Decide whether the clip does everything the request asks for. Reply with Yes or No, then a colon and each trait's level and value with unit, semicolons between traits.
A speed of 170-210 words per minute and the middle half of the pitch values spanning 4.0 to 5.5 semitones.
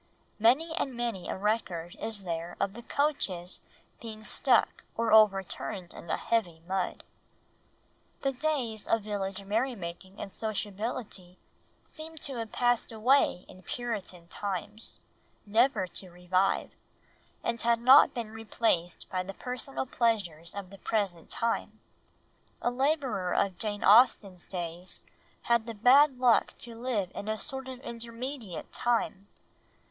No: slow, 135 wpm; average, 4.3 semitones